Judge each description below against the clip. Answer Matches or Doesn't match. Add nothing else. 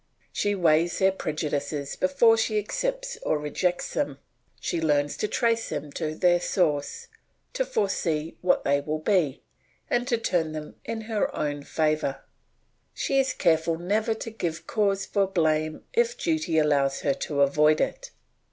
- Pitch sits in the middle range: Matches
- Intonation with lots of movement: Matches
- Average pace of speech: Matches